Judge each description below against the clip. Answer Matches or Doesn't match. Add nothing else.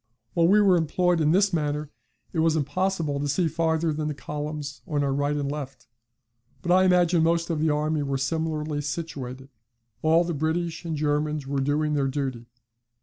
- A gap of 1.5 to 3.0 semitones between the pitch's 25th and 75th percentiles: Matches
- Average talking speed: Matches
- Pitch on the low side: Doesn't match